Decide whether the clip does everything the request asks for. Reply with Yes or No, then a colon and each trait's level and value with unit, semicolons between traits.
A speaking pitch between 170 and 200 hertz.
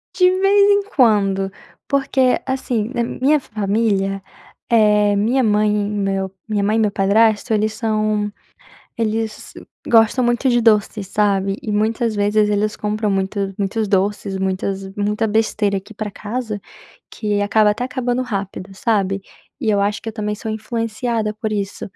No: high, 210 Hz